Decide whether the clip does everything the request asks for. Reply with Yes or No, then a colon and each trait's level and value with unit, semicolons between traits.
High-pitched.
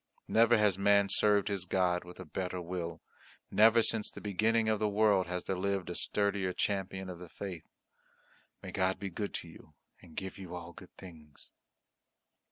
No: very low, 95 Hz